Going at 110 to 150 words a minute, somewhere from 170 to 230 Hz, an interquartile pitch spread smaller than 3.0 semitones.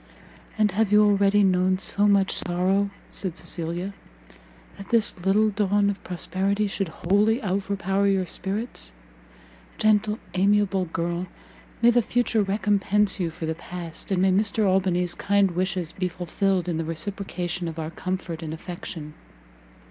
Yes: average, 145 wpm; high, 190 Hz; narrow, 2.4 semitones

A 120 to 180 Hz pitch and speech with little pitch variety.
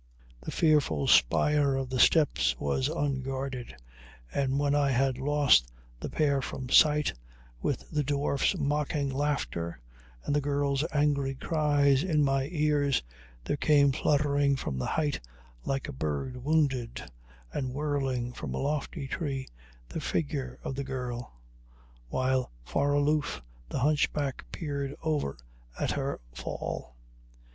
Yes: medium, 140 Hz; narrow, 2.0 semitones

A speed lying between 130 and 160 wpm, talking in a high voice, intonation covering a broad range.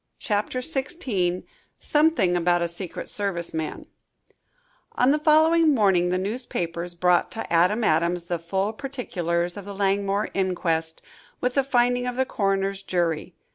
Yes: average, 140 wpm; high, 195 Hz; wide, 6.0 semitones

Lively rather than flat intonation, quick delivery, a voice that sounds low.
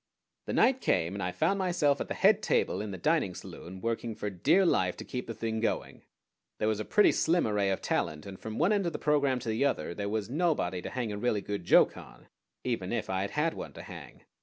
Yes: wide, 7.7 semitones; fast, 250 wpm; low, 115 Hz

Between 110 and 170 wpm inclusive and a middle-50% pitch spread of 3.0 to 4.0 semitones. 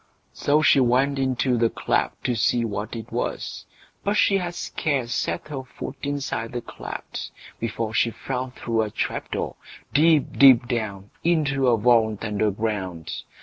Yes: average, 160 wpm; average, 3.7 semitones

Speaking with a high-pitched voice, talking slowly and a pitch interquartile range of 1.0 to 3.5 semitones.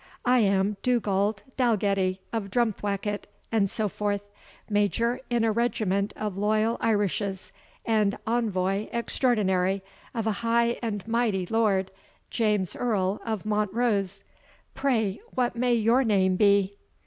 Yes: high, 210 Hz; slow, 125 wpm; average, 2.7 semitones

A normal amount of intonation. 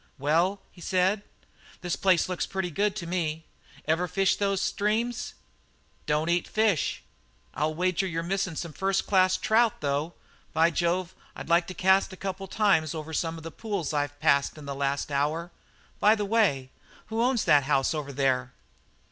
Yes: average, 4.2 semitones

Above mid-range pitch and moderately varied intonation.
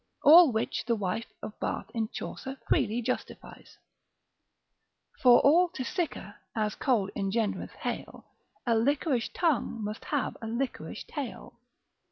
Yes: high, 235 Hz; average, 4.2 semitones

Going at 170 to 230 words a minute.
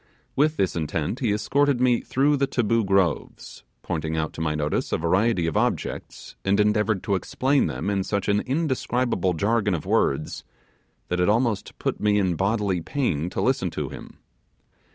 Yes: average, 175 wpm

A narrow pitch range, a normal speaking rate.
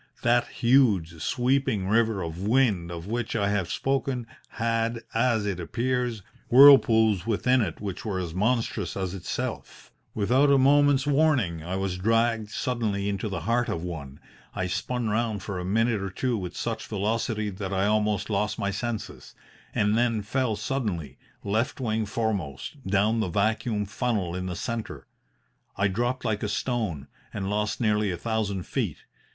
No: average, 3.6 semitones; average, 160 wpm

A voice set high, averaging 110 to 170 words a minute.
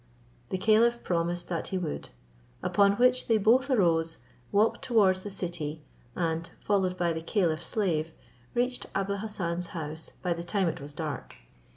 No: medium, 180 Hz; average, 160 wpm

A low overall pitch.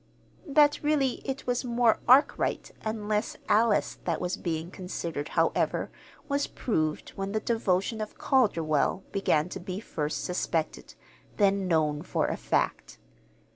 No: high, 200 Hz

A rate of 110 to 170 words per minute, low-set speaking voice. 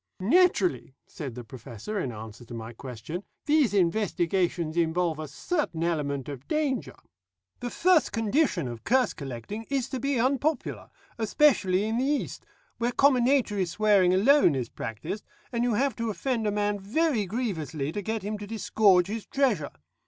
No: average, 160 wpm; high, 205 Hz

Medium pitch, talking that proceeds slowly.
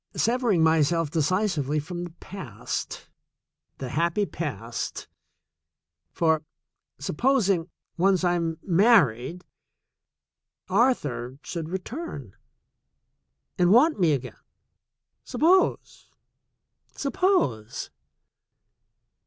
Yes: medium, 170 Hz; slow, 85 wpm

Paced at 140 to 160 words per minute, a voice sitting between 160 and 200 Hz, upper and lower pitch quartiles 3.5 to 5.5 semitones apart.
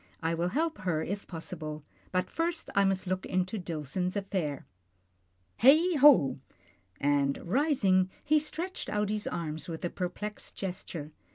Yes: average, 145 wpm; medium, 185 Hz; average, 4.8 semitones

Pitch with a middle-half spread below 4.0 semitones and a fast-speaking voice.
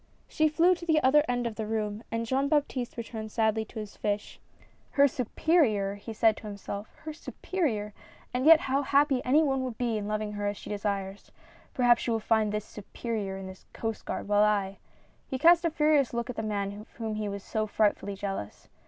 No: average, 4.3 semitones; fast, 230 wpm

